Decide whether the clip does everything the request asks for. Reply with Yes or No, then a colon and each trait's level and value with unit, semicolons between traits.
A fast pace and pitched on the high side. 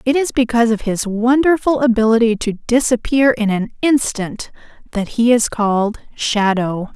No: average, 145 wpm; high, 230 Hz